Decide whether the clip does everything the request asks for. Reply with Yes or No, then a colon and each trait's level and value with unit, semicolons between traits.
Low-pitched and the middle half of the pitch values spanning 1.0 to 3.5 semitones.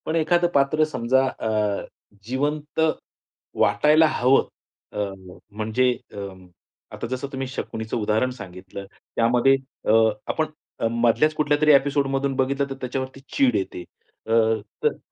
No: low, 130 Hz; average, 3.9 semitones